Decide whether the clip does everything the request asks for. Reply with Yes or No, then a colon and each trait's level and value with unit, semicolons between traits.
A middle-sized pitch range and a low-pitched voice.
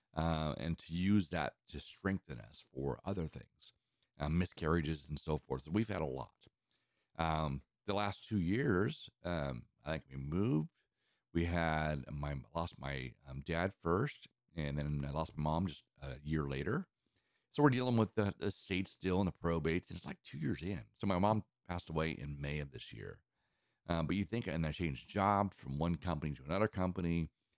Yes: average, 4.0 semitones; very low, 85 Hz